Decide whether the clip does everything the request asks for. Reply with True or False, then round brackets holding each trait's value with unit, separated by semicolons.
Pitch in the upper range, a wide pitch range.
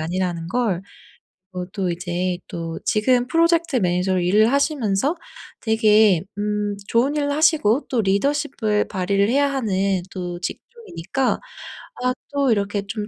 True (210 Hz; 6.2 semitones)